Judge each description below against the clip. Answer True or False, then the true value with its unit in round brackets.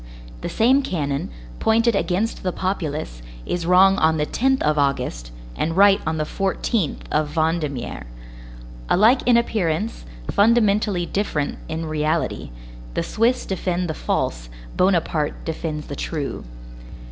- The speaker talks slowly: True (130 wpm)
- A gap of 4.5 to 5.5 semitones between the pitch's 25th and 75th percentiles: True (5.1 semitones)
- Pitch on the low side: False (175 Hz)